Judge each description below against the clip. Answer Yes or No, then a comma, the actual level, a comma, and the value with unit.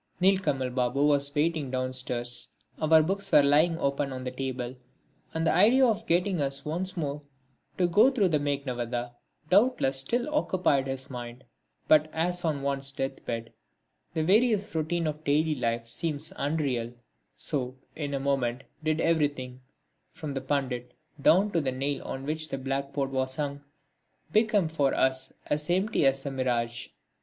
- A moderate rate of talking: Yes, average, 160 wpm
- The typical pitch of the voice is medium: Yes, medium, 145 Hz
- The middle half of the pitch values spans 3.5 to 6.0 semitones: Yes, average, 3.8 semitones